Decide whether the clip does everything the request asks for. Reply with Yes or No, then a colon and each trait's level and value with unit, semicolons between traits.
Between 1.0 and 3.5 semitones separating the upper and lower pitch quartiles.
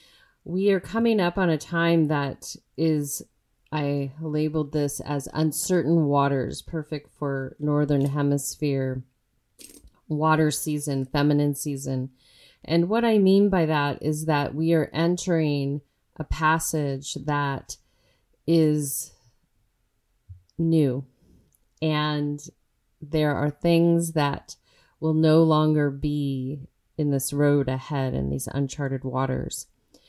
Yes: narrow, 2.6 semitones